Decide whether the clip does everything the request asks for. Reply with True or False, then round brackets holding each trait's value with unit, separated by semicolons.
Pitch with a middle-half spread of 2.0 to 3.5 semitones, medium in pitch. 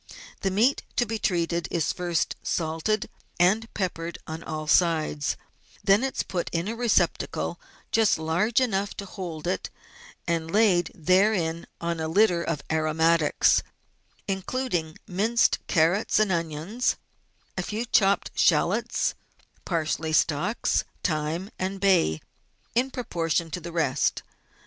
False (4.2 semitones; 175 Hz)